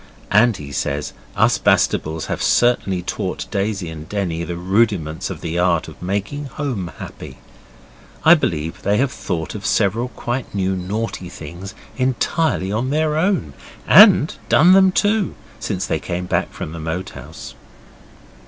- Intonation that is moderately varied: No, wide, 6.7 semitones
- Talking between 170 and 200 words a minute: No, average, 155 wpm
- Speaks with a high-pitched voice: No, low, 100 Hz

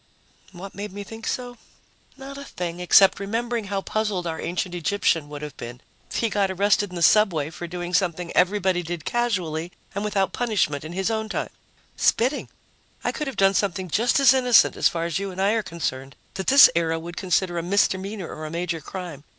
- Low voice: No, high, 190 Hz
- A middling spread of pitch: Yes, average, 3.8 semitones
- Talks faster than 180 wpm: Yes, average, 200 wpm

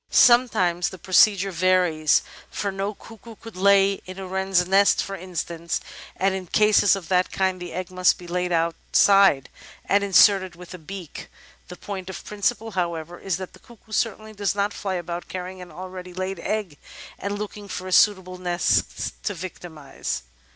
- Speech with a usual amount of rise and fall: No, narrow, 2.0 semitones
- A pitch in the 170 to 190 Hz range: Yes, medium, 185 Hz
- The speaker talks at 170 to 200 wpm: Yes, average, 175 wpm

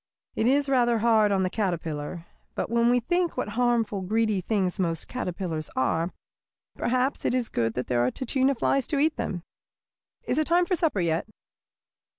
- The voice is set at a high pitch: Yes, high, 220 Hz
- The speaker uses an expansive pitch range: Yes, wide, 6.4 semitones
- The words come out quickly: No, average, 175 wpm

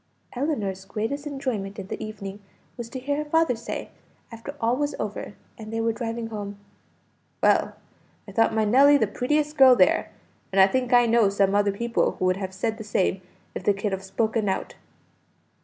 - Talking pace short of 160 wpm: No, average, 190 wpm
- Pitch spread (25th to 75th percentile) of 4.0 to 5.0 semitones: Yes, average, 4.3 semitones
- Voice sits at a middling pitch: No, high, 225 Hz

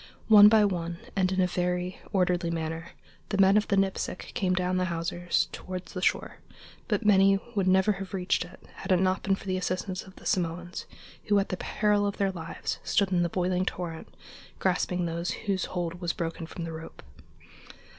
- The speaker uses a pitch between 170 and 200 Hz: Yes, medium, 185 Hz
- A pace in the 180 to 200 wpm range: Yes, average, 195 wpm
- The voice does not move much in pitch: Yes, narrow, 1.8 semitones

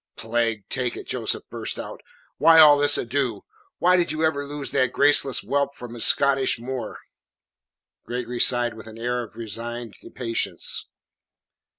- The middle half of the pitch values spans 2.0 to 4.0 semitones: Yes, average, 3.3 semitones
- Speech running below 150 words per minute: No, average, 155 wpm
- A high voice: No, low, 125 Hz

